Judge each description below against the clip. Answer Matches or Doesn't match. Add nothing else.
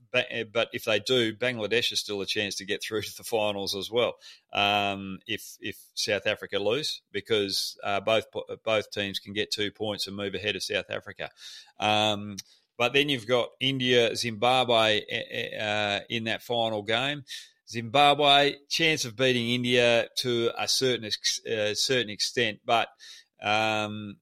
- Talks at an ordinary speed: Matches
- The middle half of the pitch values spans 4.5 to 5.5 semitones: Doesn't match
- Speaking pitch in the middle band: Doesn't match